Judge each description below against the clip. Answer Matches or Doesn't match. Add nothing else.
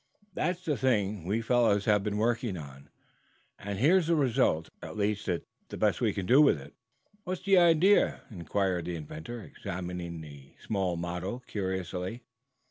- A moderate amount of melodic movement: Doesn't match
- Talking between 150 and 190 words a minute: Matches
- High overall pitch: Doesn't match